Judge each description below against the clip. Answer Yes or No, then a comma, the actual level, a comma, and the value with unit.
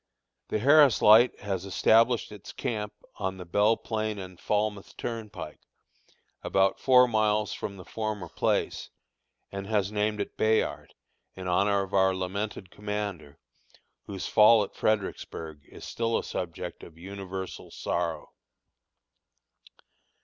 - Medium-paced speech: No, slow, 125 wpm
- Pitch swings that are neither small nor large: No, narrow, 2.3 semitones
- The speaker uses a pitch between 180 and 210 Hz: No, low, 105 Hz